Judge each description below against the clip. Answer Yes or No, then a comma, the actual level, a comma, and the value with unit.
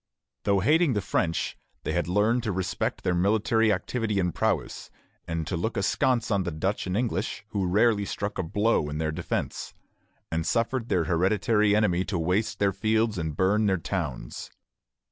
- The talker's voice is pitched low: Yes, low, 100 Hz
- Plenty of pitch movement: No, average, 3.8 semitones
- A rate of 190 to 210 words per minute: No, average, 175 wpm